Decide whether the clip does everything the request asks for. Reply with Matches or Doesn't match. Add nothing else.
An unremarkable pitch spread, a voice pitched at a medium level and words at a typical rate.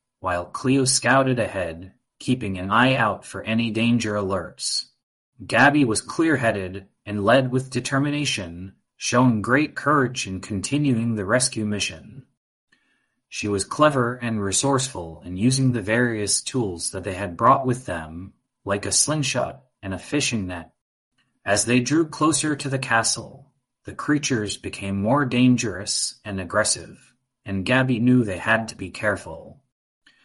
Doesn't match